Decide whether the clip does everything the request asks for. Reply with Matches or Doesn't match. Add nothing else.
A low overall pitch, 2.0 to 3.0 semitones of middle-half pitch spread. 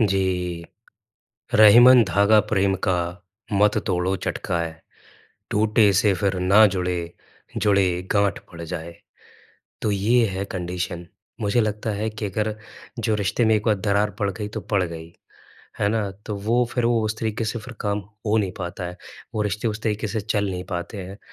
Matches